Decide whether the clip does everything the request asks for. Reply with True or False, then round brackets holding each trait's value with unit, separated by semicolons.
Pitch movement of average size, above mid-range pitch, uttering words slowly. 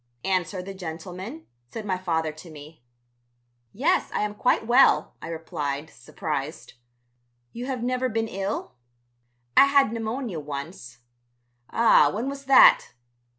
False (7.0 semitones; 195 Hz; 130 wpm)